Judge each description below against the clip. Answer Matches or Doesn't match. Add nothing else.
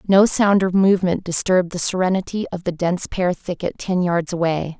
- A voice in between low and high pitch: Matches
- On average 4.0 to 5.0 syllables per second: Doesn't match